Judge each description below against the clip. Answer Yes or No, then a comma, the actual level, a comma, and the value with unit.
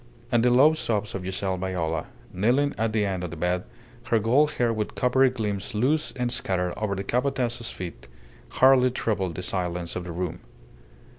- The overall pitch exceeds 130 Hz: No, low, 105 Hz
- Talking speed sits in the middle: Yes, average, 180 wpm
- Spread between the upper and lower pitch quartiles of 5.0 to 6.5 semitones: Yes, average, 5.3 semitones